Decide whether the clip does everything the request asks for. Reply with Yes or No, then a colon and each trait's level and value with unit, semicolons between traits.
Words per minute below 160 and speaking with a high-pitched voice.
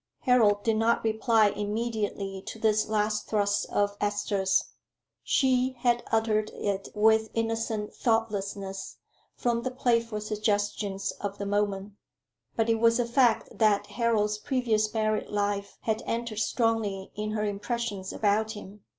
Yes: slow, 135 wpm; high, 215 Hz